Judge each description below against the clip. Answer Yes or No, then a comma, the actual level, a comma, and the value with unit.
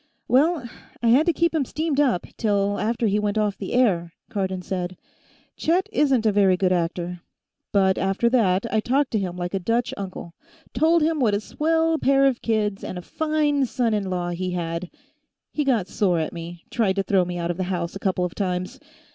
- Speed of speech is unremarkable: No, fast, 210 wpm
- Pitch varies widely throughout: Yes, wide, 6.2 semitones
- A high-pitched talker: Yes, high, 205 Hz